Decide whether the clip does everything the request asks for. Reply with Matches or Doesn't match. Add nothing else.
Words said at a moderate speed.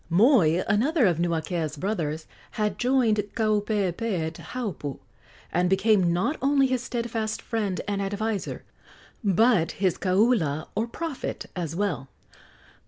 Doesn't match